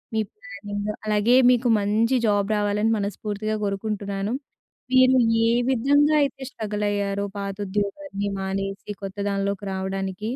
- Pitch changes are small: Yes, narrow, 1.8 semitones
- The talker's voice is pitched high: Yes, high, 205 Hz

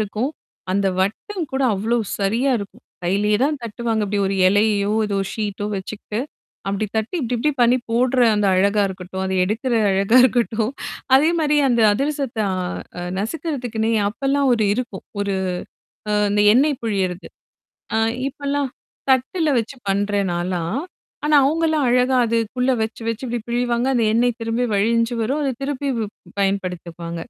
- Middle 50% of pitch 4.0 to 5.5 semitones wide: Yes, average, 4.4 semitones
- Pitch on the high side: Yes, high, 230 Hz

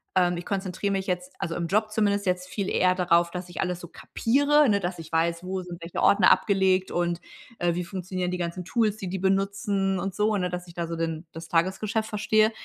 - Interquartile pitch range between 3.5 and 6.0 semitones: No, narrow, 2.4 semitones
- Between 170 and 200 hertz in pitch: Yes, medium, 185 Hz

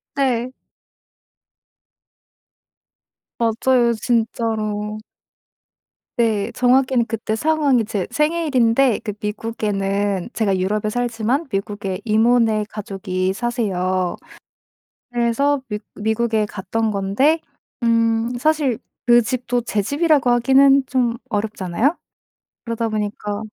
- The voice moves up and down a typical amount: Yes, average, 3.0 semitones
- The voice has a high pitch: Yes, high, 230 Hz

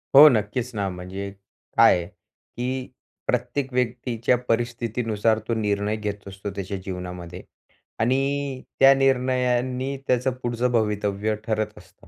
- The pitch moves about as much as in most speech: Yes, average, 3.7 semitones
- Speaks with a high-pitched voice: No, low, 115 Hz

